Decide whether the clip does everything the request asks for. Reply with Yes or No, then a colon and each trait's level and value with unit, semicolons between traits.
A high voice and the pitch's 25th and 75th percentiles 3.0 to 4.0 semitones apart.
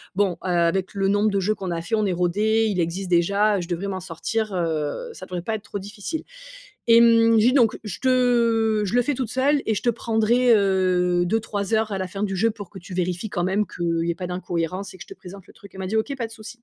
Yes: high, 200 Hz; average, 3.7 semitones